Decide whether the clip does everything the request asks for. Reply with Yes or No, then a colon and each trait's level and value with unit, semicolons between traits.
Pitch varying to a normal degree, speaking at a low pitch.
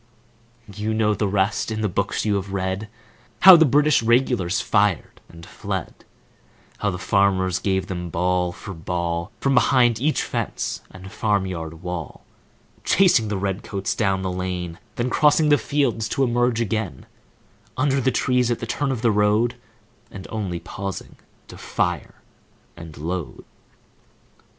Yes: average, 4.6 semitones; low, 100 Hz